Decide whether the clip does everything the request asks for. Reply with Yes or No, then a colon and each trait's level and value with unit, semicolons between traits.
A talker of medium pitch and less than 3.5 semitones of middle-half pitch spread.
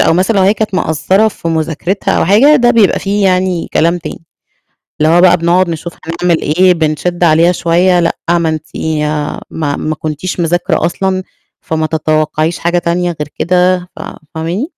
Yes: medium, 175 Hz; narrow, 2.5 semitones